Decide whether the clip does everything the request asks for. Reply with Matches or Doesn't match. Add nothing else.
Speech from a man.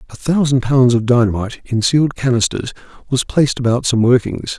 Matches